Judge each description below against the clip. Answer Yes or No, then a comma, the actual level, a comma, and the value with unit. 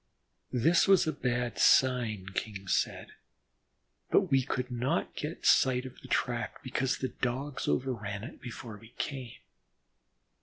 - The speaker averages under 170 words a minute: Yes, average, 140 wpm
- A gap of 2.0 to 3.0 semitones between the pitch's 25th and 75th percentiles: Yes, narrow, 2.4 semitones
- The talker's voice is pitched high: No, low, 125 Hz